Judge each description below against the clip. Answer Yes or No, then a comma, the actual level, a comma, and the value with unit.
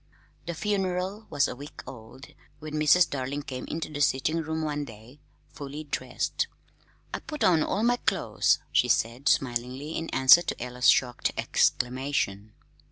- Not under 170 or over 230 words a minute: No, average, 155 wpm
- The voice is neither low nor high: Yes, medium, 145 Hz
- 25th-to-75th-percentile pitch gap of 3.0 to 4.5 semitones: Yes, average, 4.2 semitones